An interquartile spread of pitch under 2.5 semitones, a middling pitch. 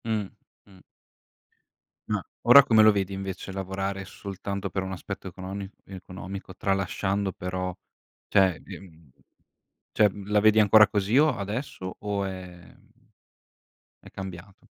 No: narrow, 1.7 semitones; very low, 95 Hz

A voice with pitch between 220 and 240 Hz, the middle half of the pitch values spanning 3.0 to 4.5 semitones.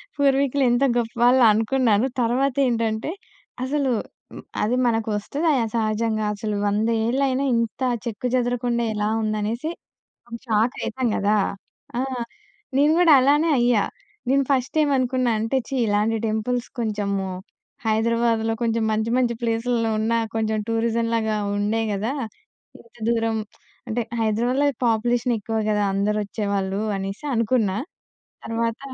No: high, 230 Hz; narrow, 2.4 semitones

